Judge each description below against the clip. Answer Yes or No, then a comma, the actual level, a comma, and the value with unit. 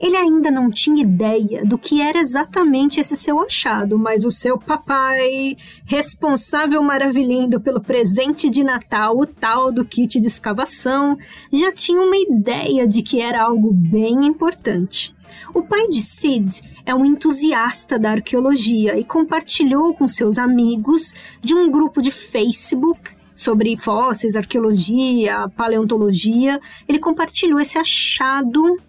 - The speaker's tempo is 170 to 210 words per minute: No, average, 135 wpm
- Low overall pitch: No, very high, 265 Hz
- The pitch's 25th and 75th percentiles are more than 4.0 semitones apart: Yes, average, 5.0 semitones